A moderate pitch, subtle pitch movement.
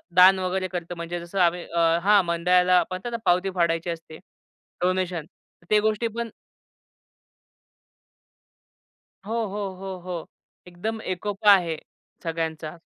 Yes: medium, 180 Hz; narrow, 2.3 semitones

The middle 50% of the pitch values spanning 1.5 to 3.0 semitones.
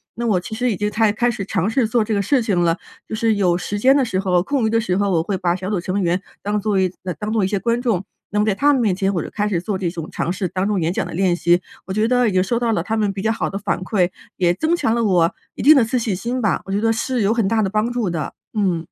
No: average, 3.5 semitones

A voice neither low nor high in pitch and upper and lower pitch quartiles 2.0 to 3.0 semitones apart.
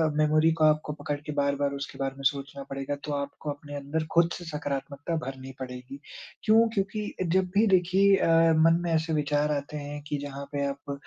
Yes: medium, 145 Hz; average, 2.7 semitones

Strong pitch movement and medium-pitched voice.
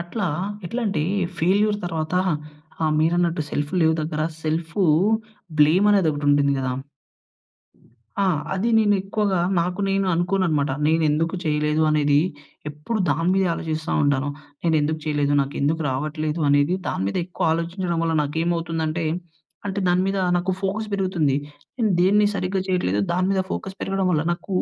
No: average, 3.9 semitones; medium, 165 Hz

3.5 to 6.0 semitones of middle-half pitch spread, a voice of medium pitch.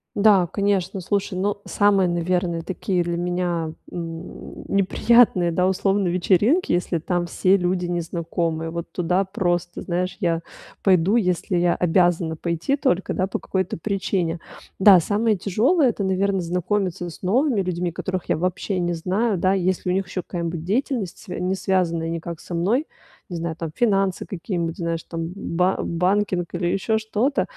No: narrow, 2.4 semitones; medium, 180 Hz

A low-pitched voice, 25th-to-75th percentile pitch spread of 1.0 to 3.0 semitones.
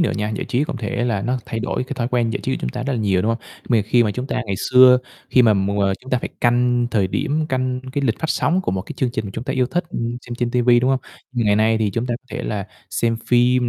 Yes: low, 120 Hz; narrow, 2.6 semitones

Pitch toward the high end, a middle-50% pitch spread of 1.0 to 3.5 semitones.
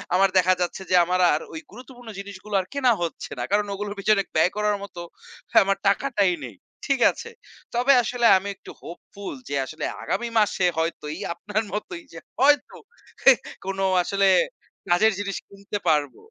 Yes: high, 200 Hz; average, 3.2 semitones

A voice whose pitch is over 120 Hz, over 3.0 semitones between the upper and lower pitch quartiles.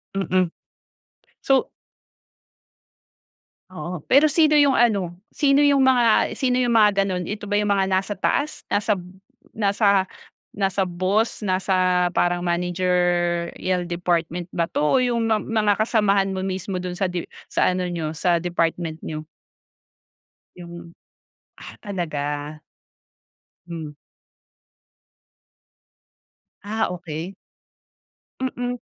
Yes: medium, 185 Hz; average, 3.5 semitones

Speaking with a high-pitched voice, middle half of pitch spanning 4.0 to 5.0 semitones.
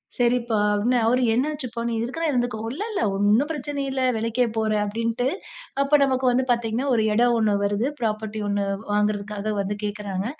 No: high, 230 Hz; average, 3.3 semitones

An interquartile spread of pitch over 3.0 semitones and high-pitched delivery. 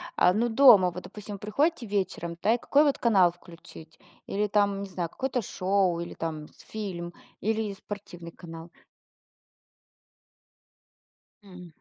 Yes: average, 3.7 semitones; high, 195 Hz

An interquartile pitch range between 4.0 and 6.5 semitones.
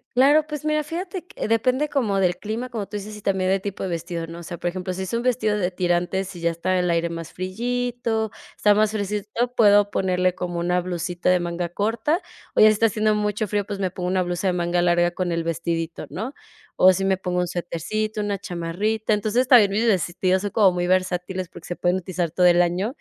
No: average, 3.4 semitones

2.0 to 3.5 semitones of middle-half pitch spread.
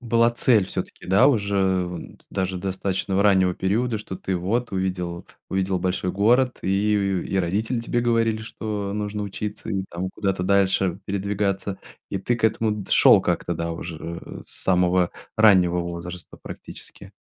Yes: narrow, 2.5 semitones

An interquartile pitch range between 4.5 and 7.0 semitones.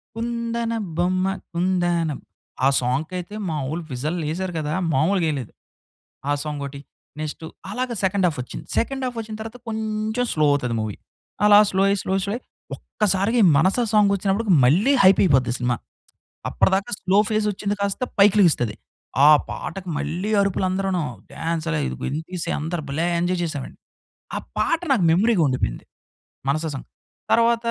Yes: average, 5.3 semitones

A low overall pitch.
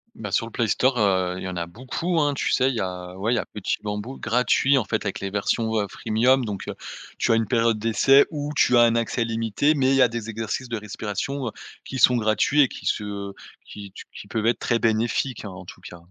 Yes: low, 115 Hz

